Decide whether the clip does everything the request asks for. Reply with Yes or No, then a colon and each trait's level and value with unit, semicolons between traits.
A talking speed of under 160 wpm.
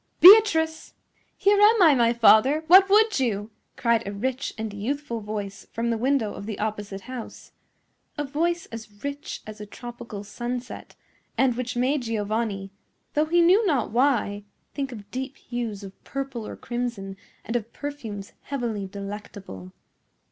Yes: average, 150 wpm